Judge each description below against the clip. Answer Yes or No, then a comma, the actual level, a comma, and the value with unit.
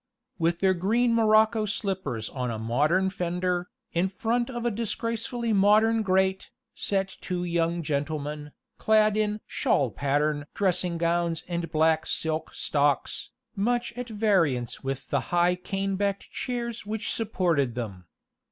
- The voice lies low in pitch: No, medium, 185 Hz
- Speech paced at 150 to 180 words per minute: No, slow, 135 wpm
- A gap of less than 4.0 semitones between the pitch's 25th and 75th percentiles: No, wide, 5.4 semitones